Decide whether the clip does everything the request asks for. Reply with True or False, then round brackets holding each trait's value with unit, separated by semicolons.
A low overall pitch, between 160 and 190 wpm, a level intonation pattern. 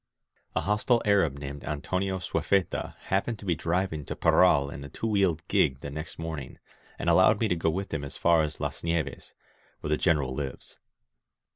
False (80 Hz; 185 wpm; 4.8 semitones)